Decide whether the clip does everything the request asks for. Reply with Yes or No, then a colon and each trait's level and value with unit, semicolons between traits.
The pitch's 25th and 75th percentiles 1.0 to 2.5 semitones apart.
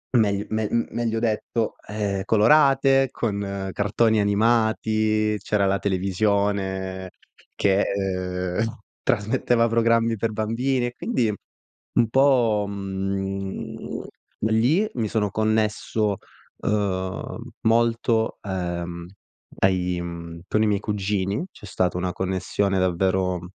No: average, 2.9 semitones